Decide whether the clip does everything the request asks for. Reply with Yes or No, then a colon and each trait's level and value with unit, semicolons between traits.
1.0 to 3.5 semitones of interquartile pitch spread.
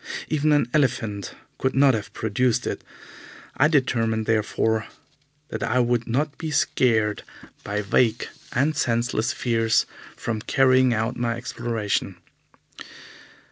Yes: average, 3.0 semitones